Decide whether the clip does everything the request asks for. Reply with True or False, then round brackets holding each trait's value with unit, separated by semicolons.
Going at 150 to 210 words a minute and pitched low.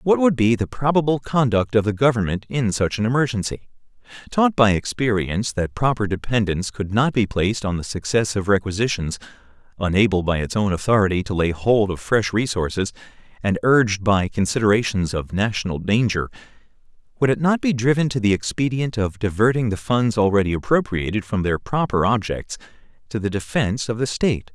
True (170 wpm; 110 Hz)